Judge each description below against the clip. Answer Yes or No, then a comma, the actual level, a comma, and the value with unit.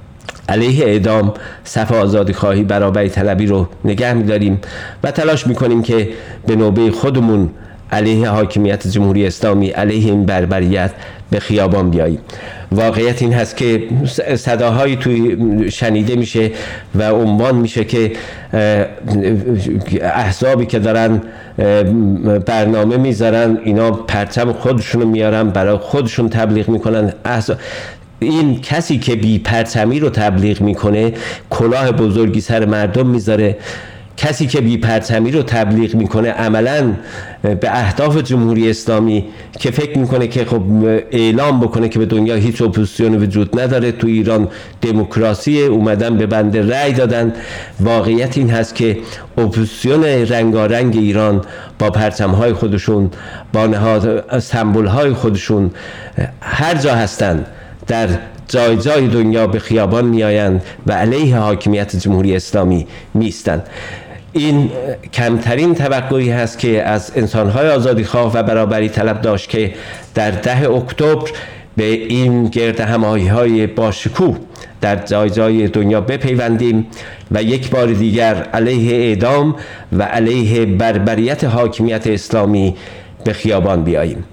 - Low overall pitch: Yes, low, 110 Hz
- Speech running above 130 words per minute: No, average, 120 wpm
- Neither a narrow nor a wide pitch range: No, narrow, 2.1 semitones